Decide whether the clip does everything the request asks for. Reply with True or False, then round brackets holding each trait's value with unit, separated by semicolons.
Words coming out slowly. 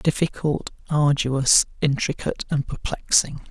True (85 wpm)